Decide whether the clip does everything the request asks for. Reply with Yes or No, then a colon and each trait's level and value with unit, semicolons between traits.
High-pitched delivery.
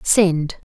No: medium, 170 Hz